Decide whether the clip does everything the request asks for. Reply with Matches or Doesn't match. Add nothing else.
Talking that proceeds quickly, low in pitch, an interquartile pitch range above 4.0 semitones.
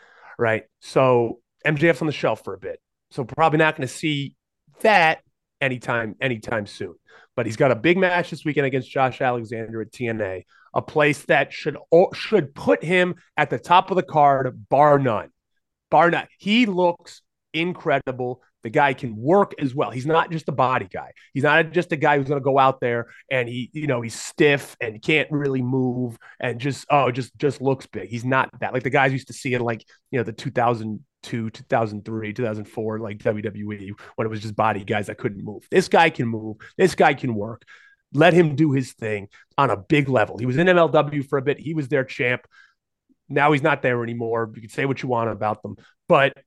Matches